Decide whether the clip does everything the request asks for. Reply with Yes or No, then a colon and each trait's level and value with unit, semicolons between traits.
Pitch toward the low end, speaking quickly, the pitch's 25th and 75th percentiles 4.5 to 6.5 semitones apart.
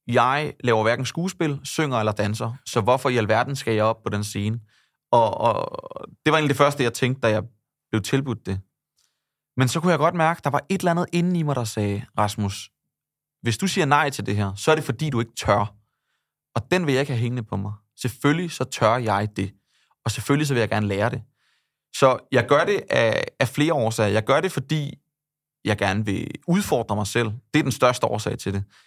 Yes: low, 125 Hz; fast, 230 wpm; wide, 5.6 semitones